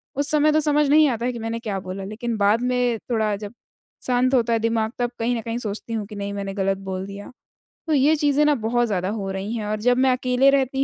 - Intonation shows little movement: No, average, 3.7 semitones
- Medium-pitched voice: No, high, 230 Hz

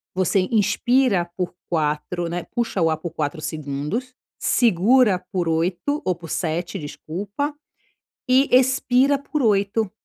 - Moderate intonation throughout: No, wide, 6.8 semitones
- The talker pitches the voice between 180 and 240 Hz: Yes, high, 190 Hz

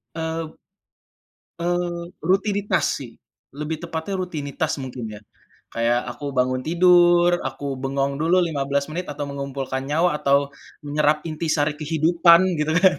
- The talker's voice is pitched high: No, medium, 155 Hz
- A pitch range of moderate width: Yes, average, 3.7 semitones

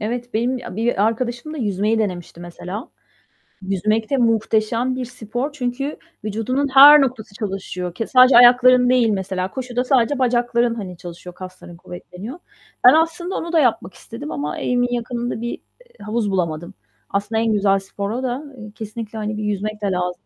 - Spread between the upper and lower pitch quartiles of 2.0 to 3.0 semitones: No, average, 4.0 semitones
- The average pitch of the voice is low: No, high, 225 Hz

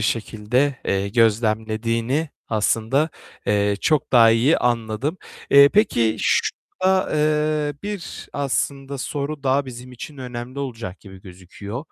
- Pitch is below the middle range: Yes, low, 125 Hz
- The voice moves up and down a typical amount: Yes, average, 4.5 semitones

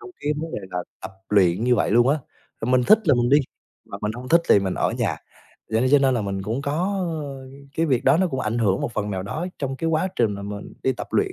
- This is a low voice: Yes, low, 125 Hz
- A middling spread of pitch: No, wide, 5.9 semitones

